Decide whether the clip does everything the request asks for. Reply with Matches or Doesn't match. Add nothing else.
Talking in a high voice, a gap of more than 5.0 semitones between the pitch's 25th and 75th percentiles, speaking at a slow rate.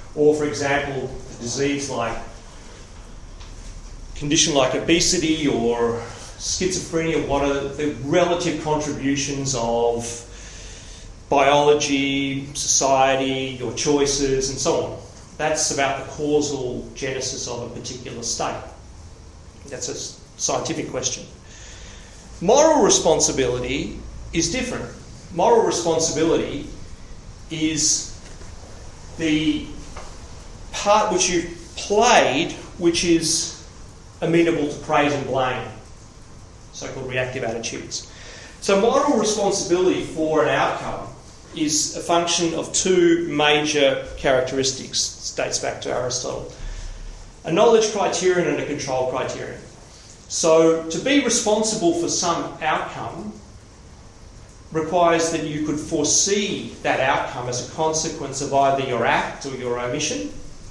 Doesn't match